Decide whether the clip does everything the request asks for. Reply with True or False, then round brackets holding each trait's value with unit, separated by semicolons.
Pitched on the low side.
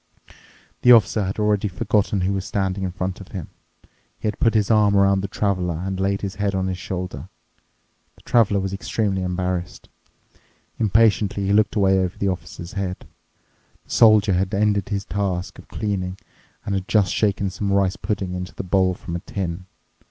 True (95 Hz)